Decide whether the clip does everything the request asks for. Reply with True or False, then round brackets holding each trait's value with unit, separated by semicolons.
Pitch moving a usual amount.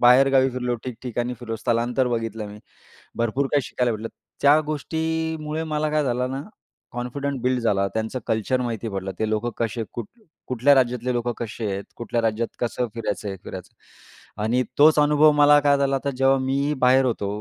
True (3.5 semitones)